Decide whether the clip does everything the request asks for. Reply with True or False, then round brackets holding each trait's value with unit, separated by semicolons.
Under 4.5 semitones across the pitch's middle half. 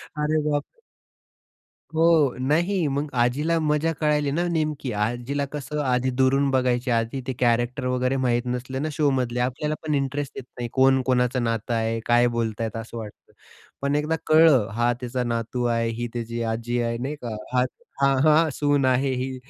True (3.4 semitones)